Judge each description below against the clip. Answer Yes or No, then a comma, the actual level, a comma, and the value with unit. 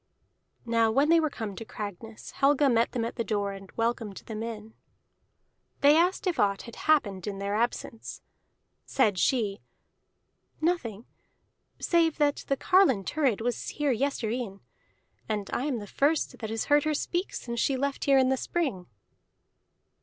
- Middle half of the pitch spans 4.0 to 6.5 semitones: Yes, average, 5.2 semitones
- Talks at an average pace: Yes, average, 160 wpm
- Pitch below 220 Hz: No, high, 235 Hz